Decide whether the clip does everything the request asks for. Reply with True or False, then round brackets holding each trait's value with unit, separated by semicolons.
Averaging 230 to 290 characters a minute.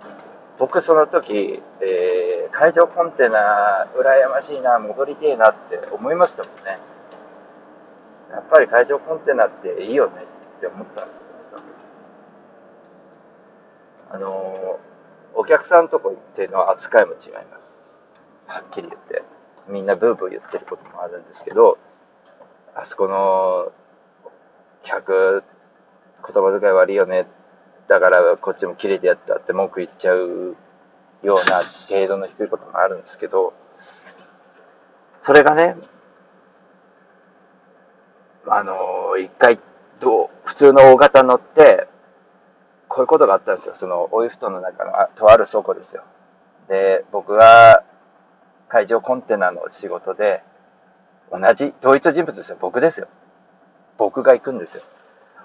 True (260 characters per minute)